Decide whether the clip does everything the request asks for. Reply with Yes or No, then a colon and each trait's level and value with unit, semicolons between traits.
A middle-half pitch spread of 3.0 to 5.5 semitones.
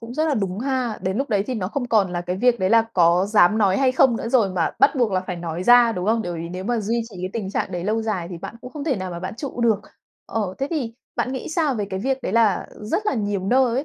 Yes: average, 4.8 semitones